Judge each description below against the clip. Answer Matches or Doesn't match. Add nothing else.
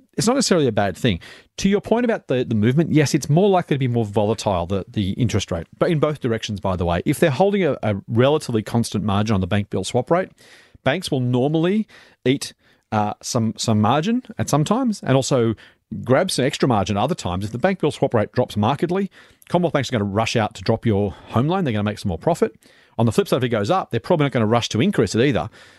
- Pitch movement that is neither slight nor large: Doesn't match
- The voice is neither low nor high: Doesn't match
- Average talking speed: Doesn't match